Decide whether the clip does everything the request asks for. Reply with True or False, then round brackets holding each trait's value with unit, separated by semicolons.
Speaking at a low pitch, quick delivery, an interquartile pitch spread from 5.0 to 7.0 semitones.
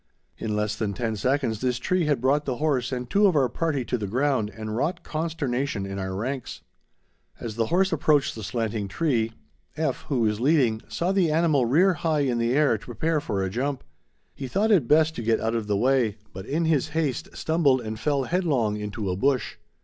True (130 Hz; 210 wpm; 5.6 semitones)